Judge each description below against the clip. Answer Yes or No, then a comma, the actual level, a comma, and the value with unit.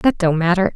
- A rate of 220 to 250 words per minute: Yes, fast, 235 wpm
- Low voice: No, medium, 185 Hz